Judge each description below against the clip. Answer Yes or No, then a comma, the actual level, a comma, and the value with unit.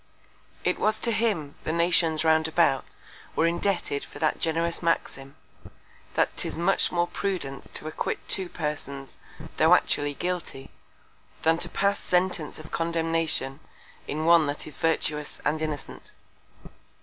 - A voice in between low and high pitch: Yes, medium, 160 Hz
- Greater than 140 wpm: No, slow, 135 wpm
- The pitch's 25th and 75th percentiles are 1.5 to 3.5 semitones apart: Yes, narrow, 2.5 semitones